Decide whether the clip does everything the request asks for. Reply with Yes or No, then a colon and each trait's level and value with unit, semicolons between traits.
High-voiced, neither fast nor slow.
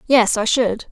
Yes: high, 230 Hz; average, 195 wpm